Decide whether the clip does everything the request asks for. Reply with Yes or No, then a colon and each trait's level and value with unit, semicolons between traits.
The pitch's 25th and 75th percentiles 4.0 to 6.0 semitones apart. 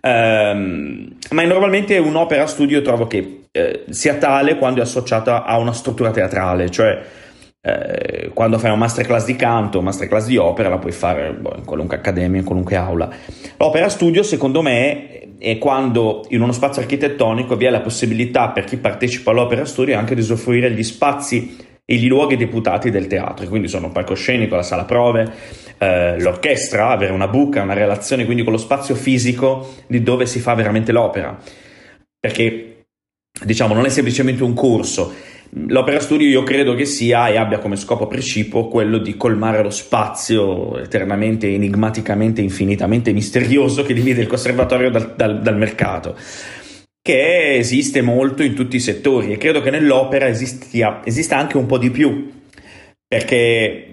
No: average, 3.6 semitones